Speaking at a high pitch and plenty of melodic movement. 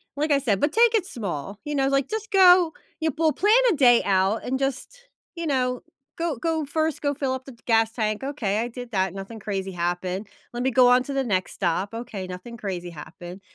Yes: high, 245 Hz; wide, 6.8 semitones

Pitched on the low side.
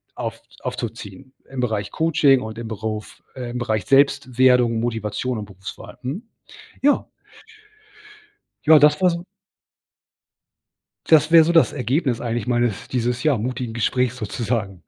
Yes: low, 125 Hz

